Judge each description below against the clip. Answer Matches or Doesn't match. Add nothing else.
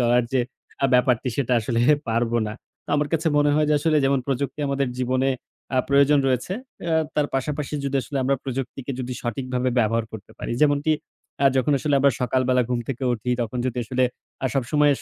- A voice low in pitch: Matches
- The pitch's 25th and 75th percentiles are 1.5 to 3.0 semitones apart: Matches